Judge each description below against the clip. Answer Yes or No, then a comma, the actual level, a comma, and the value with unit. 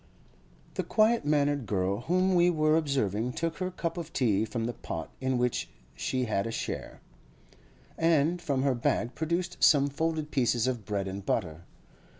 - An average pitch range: No, wide, 6.4 semitones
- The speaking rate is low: No, average, 165 wpm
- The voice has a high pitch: No, low, 135 Hz